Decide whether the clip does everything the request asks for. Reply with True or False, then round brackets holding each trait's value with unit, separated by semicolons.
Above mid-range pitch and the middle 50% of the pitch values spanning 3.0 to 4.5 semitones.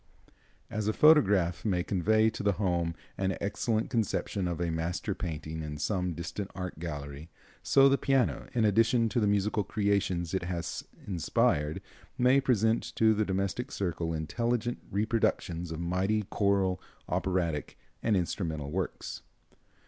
False (95 Hz; 4.2 semitones)